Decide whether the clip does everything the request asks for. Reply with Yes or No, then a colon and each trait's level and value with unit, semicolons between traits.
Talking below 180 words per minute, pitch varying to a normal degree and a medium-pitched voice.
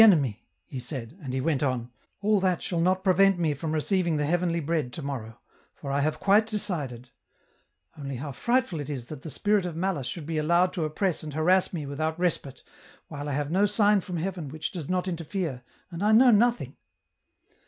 No: fast, 205 wpm; average, 4.8 semitones; medium, 165 Hz